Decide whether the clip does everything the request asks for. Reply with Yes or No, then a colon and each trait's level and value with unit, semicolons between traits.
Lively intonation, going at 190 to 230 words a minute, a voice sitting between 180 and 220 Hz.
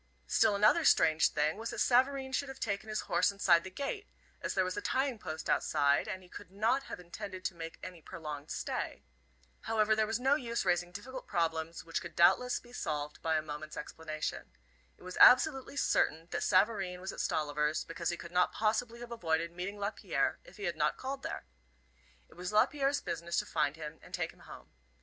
Yes: wide, 6.2 semitones; fast, 205 wpm; medium, 185 Hz